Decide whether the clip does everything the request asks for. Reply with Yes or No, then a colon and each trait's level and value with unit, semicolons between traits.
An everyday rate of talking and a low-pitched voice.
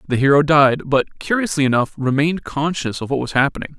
No: average, 190 wpm; medium, 145 Hz